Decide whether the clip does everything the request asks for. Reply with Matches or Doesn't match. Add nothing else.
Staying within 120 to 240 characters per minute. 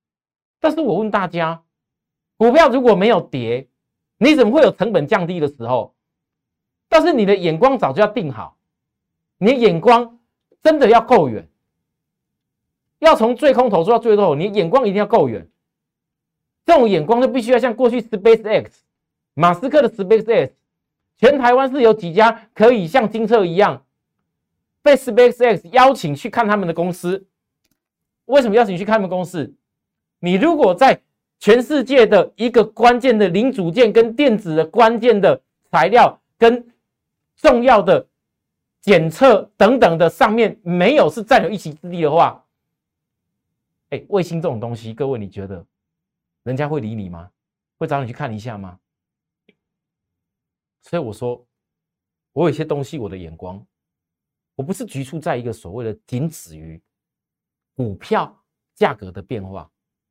Matches